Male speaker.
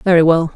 No: female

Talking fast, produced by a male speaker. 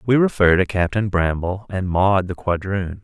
No: average, 180 wpm; male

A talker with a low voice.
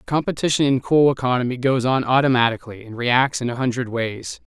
Yes: low, 125 Hz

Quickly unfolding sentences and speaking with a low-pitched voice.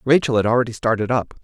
Yes: fast, 210 wpm; low, 120 Hz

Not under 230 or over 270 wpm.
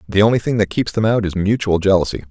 Yes: fast, 260 wpm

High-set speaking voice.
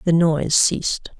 No: medium, 165 Hz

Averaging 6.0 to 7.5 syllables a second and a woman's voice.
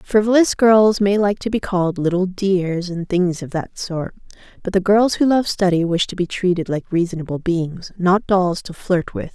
No: 4.8 syllables/s; female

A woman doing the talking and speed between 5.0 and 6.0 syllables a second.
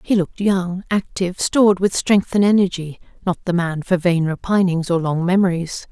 Yes: female; 5.2 syllables/s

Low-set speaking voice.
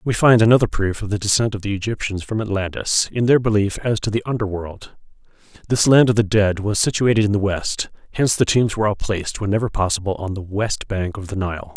Yes: low, 105 Hz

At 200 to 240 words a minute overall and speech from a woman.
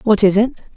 Yes: fast, 235 wpm; female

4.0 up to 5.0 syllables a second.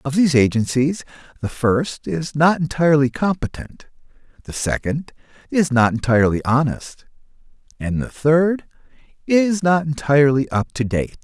Yes: 4.8 syllables/s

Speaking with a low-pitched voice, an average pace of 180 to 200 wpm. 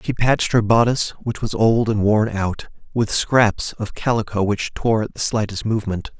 Yes: low, 110 Hz; average, 195 wpm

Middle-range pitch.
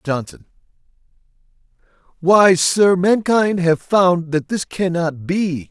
Yes: medium, 175 Hz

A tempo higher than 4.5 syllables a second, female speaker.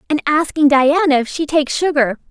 Yes: 5.6 syllables/s; female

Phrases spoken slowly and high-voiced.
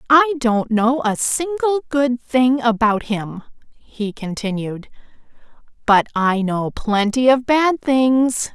Yes: slow, 125 wpm; high, 240 Hz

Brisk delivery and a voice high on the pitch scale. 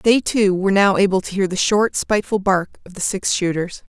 Yes: fast, 230 wpm; high, 195 Hz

